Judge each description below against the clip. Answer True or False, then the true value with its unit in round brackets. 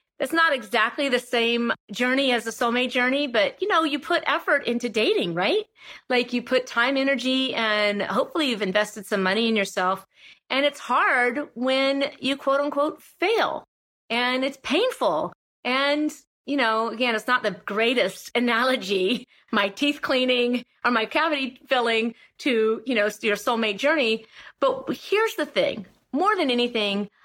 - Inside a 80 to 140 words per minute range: False (160 wpm)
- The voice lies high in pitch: True (250 Hz)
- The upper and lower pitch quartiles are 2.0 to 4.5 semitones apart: True (4.1 semitones)